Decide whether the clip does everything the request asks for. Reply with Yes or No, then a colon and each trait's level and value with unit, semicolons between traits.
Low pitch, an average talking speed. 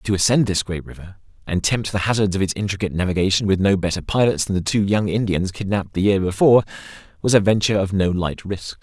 No: low, 100 Hz; fast, 225 wpm